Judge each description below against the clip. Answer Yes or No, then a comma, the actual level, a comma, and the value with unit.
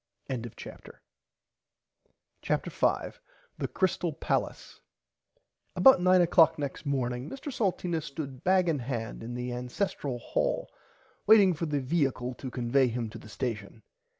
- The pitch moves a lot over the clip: Yes, wide, 6.2 semitones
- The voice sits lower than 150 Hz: Yes, medium, 140 Hz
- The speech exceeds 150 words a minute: No, slow, 135 wpm